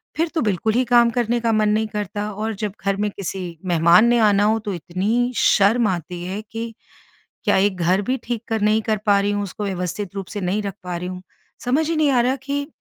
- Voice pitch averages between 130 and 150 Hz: No, high, 210 Hz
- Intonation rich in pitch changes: No, average, 3.4 semitones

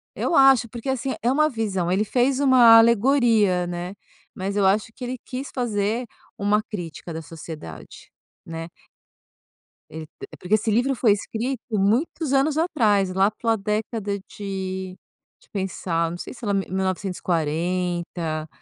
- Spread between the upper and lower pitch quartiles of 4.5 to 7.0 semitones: Yes, average, 4.9 semitones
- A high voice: Yes, high, 205 Hz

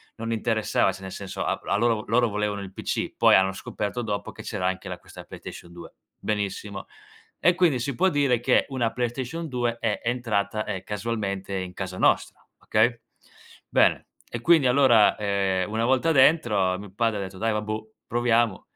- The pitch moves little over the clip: No, average, 3.4 semitones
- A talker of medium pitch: No, low, 110 Hz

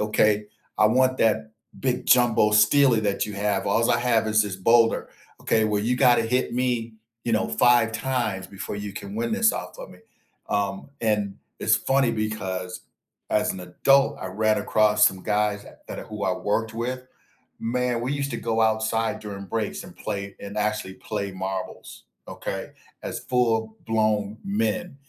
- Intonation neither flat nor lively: Yes, average, 3.0 semitones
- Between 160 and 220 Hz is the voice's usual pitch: No, low, 110 Hz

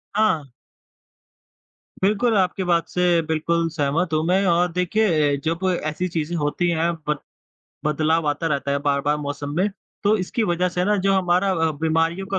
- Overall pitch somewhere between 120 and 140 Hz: No, medium, 170 Hz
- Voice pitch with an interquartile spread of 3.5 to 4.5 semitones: No, average, 3.1 semitones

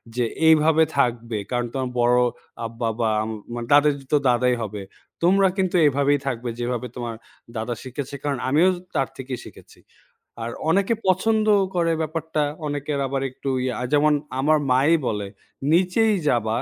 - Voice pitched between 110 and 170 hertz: Yes, low, 135 Hz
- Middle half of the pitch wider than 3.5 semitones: Yes, average, 4.7 semitones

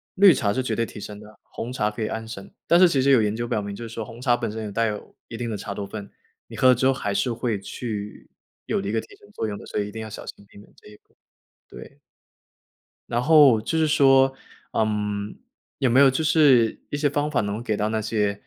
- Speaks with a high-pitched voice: No, low, 115 Hz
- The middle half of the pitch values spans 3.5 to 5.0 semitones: Yes, average, 3.9 semitones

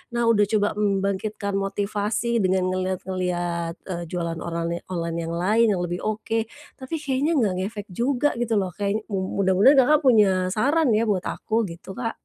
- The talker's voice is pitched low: No, high, 200 Hz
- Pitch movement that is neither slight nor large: Yes, average, 3.7 semitones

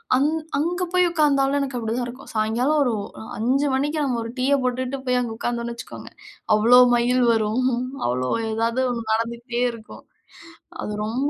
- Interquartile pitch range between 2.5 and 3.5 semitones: Yes, average, 3.0 semitones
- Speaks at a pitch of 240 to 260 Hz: Yes, high, 245 Hz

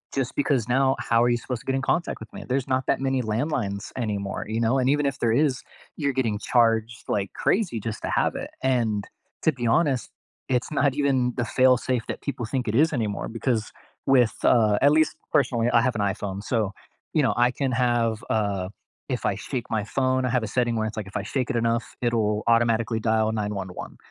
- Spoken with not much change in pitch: No, average, 3.1 semitones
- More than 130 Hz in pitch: No, low, 120 Hz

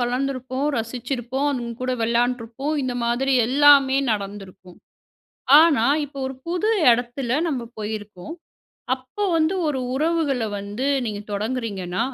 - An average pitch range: Yes, average, 3.5 semitones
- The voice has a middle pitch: No, very high, 250 Hz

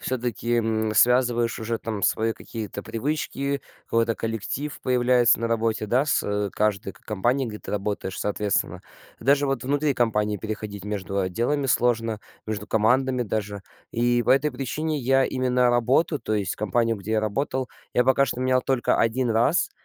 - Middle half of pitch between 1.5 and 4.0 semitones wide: Yes, average, 3.2 semitones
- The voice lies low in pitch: Yes, low, 115 Hz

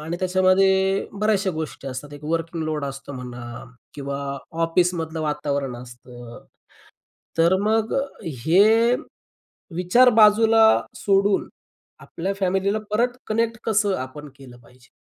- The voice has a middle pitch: Yes, medium, 170 Hz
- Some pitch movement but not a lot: No, wide, 6.4 semitones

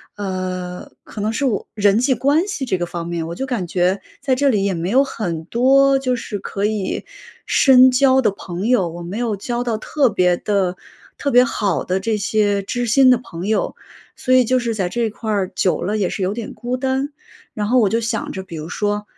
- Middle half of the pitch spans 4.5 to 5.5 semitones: Yes, average, 5.0 semitones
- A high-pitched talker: Yes, high, 215 Hz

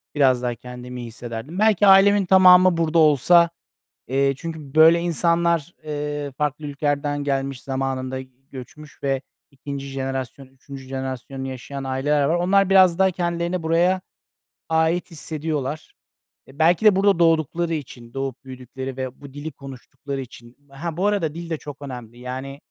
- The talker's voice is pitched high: No, medium, 145 Hz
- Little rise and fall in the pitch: No, average, 4.1 semitones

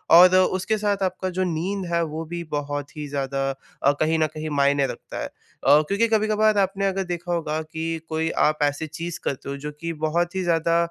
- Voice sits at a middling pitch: Yes, medium, 165 Hz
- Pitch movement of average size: Yes, average, 3.7 semitones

